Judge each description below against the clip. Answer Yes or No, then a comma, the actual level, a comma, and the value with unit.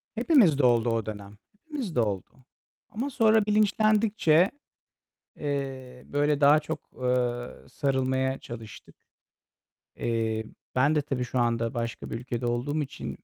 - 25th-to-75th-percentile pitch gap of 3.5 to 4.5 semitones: No, average, 5.0 semitones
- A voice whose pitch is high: No, low, 130 Hz